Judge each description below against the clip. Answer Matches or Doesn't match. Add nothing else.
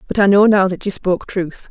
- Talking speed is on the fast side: Matches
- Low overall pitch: Doesn't match